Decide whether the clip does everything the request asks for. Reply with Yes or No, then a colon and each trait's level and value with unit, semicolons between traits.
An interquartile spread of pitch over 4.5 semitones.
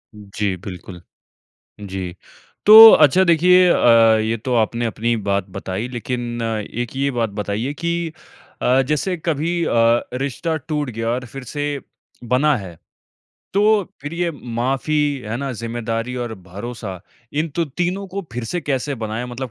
Yes: average, 5.3 semitones